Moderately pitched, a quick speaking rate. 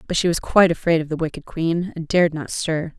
Yes: medium, 165 Hz; fast, 260 wpm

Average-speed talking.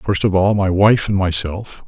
No: fast, 225 wpm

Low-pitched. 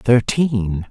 Yes: low, 115 Hz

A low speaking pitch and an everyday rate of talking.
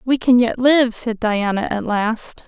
No: high, 230 Hz; average, 195 wpm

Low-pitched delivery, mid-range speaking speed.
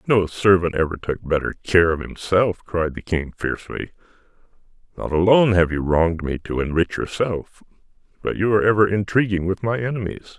Yes: very low, 95 Hz; average, 170 wpm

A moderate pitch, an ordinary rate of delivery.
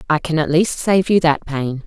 No: medium, 160 Hz; fast, 255 wpm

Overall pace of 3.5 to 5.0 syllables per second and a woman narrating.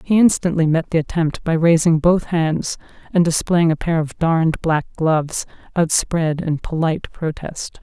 Yes: 4.6 syllables/s; female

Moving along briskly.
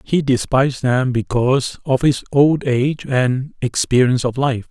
No: average, 155 wpm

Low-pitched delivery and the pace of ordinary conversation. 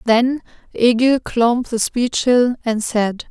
No: high, 240 Hz; average, 145 wpm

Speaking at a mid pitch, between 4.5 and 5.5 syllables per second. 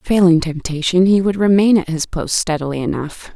Yes: medium, 175 Hz; 5.1 syllables/s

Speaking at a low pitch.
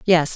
No: medium, 165 Hz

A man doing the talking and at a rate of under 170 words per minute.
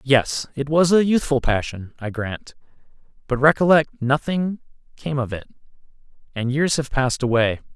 Yes: male; average, 145 wpm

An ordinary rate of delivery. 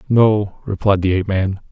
Yes: average, 175 wpm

